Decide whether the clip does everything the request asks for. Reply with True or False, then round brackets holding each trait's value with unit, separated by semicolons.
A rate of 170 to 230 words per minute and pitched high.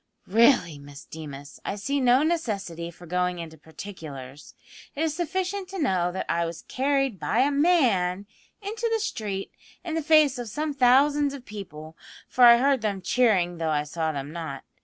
True (180 wpm; 210 Hz)